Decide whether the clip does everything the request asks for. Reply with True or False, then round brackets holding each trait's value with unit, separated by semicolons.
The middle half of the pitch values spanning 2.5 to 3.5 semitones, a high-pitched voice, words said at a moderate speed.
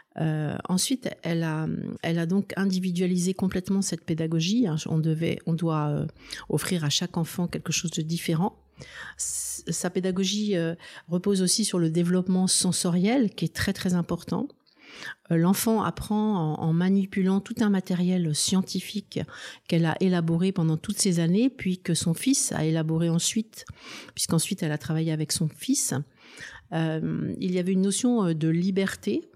False (2.9 semitones; 180 Hz; 160 wpm)